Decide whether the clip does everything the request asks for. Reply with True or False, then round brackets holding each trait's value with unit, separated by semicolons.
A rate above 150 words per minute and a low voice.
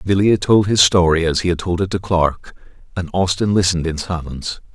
True (200 wpm; 90 Hz)